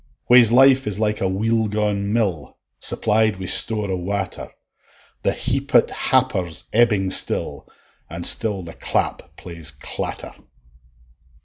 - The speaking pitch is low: Yes, low, 100 Hz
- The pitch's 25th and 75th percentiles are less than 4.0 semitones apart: Yes, average, 3.1 semitones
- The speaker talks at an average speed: No, slow, 125 wpm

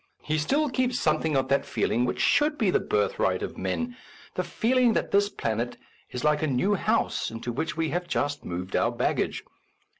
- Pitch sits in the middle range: Yes, medium, 160 Hz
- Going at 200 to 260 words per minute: Yes, fast, 205 wpm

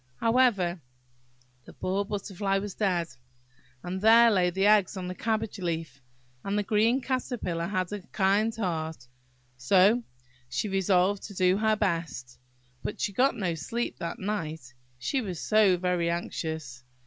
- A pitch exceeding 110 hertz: Yes, high, 190 Hz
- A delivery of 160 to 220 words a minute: No, average, 150 wpm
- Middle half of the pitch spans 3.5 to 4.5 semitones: Yes, average, 3.8 semitones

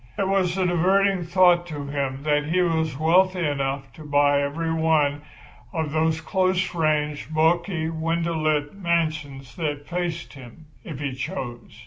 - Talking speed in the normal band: Yes, average, 150 wpm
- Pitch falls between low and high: Yes, medium, 160 Hz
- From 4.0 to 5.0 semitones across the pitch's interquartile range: No, average, 3.1 semitones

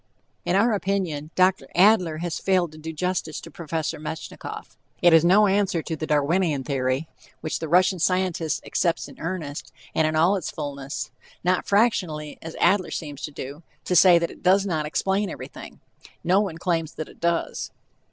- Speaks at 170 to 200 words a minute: Yes, average, 180 wpm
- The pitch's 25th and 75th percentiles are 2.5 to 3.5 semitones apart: Yes, average, 3.1 semitones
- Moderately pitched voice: Yes, medium, 170 Hz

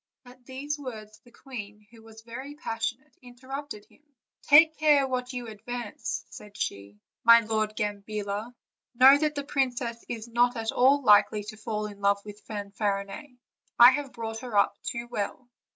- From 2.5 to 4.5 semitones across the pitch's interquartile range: Yes, average, 3.5 semitones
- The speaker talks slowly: No, average, 165 wpm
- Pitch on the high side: Yes, high, 235 Hz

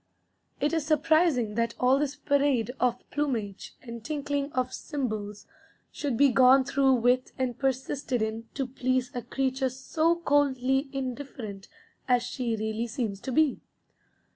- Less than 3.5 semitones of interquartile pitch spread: Yes, average, 3.0 semitones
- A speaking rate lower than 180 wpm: Yes, average, 140 wpm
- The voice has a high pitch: Yes, very high, 260 Hz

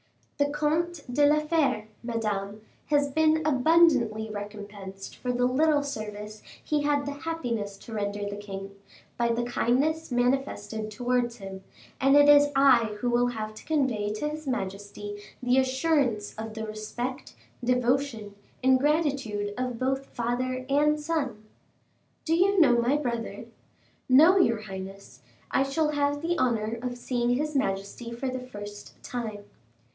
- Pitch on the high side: Yes, high, 245 Hz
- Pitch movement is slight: No, average, 5.1 semitones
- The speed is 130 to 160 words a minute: Yes, average, 150 wpm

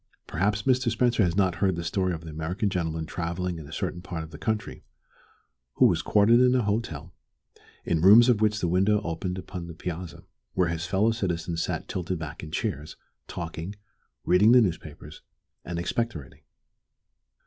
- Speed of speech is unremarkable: Yes, average, 180 wpm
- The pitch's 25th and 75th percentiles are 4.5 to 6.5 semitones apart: No, average, 4.1 semitones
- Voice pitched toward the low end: Yes, very low, 90 Hz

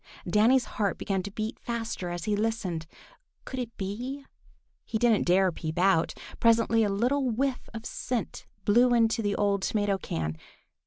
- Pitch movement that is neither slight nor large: Yes, average, 3.4 semitones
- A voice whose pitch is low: No, high, 215 Hz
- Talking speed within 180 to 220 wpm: No, average, 160 wpm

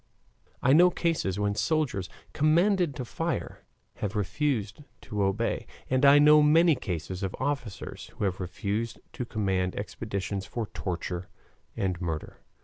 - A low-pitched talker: Yes, low, 105 Hz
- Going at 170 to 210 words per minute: No, average, 140 wpm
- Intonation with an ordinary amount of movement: No, wide, 7.4 semitones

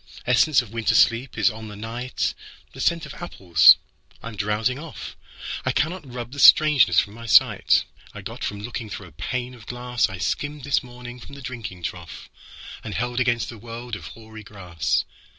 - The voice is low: Yes, low, 120 Hz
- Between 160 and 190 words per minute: Yes, average, 170 wpm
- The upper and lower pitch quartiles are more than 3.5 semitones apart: No, average, 2.9 semitones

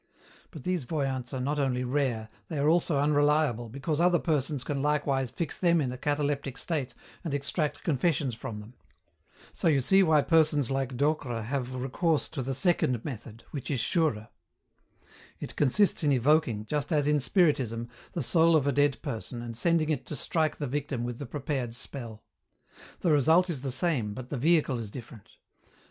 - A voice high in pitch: No, medium, 140 Hz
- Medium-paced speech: Yes, average, 180 wpm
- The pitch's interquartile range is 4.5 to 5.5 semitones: No, average, 3.7 semitones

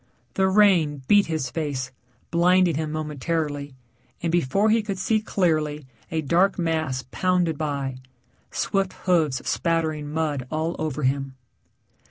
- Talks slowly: Yes, slow, 130 wpm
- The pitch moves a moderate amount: Yes, average, 3.7 semitones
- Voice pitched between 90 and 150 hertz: No, medium, 160 Hz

